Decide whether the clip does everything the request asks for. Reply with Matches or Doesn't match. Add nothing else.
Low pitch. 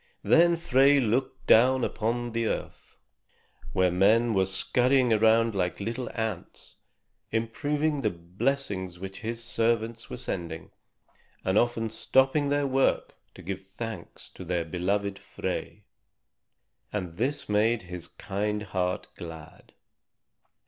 Matches